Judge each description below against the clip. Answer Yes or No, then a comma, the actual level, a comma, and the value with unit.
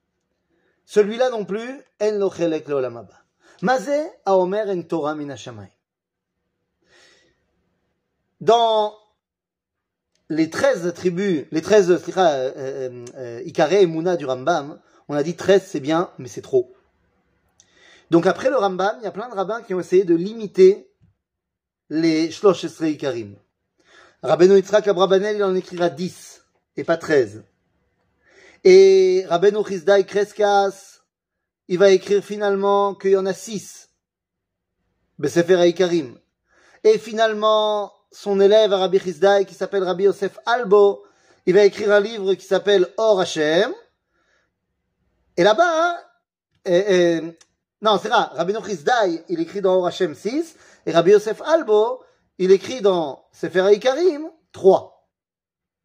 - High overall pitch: Yes, high, 195 Hz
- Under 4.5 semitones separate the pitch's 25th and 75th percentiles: Yes, average, 3.8 semitones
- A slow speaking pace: Yes, slow, 130 wpm